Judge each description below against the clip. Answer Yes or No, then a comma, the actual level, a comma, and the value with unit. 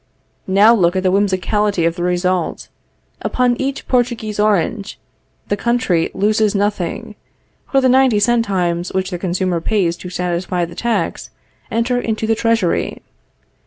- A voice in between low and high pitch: No, high, 200 Hz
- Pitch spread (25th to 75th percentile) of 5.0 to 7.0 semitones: No, average, 4.2 semitones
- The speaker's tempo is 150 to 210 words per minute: No, average, 140 wpm